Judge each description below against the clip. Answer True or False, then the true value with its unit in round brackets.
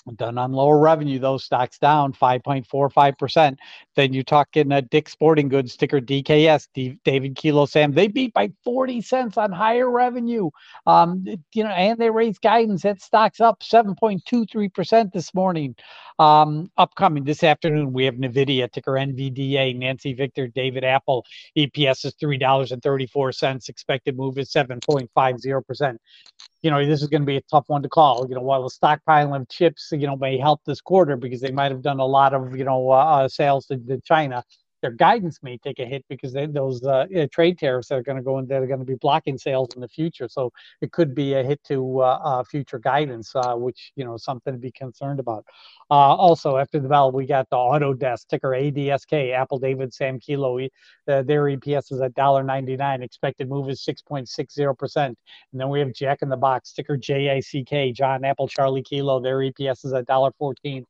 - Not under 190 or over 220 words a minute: True (200 wpm)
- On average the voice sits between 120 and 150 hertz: True (140 Hz)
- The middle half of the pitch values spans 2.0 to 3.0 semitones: True (2.4 semitones)